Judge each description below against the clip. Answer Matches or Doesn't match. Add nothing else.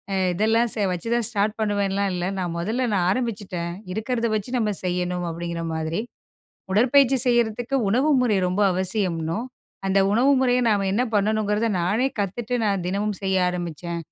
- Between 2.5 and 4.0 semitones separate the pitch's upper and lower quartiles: Doesn't match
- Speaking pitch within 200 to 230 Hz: Matches